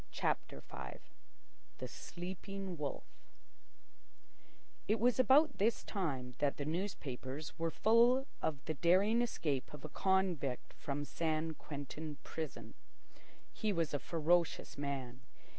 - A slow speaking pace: Yes, slow, 120 wpm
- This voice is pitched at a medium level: Yes, medium, 160 Hz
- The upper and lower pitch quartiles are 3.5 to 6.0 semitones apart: Yes, wide, 5.5 semitones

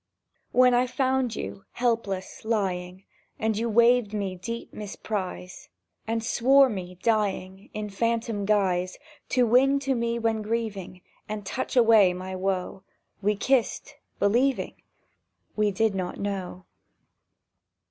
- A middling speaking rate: No, slow, 125 wpm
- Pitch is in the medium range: No, high, 215 Hz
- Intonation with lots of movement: No, average, 3.6 semitones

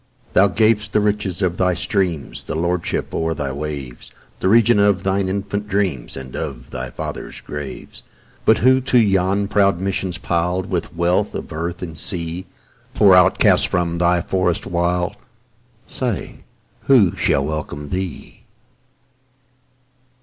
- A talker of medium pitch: No, very low, 90 Hz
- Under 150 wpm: Yes, average, 140 wpm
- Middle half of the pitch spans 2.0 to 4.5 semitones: Yes, average, 3.2 semitones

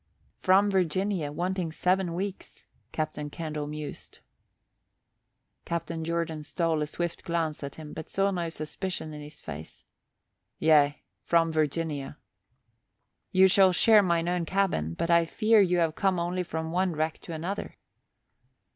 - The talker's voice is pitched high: No, medium, 170 Hz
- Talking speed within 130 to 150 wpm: Yes, average, 140 wpm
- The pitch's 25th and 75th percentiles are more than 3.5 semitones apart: No, average, 3.1 semitones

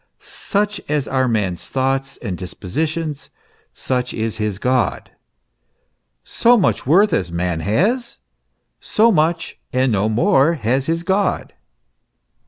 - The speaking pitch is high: No, low, 135 Hz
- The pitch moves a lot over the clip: Yes, wide, 7.7 semitones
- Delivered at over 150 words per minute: No, slow, 135 wpm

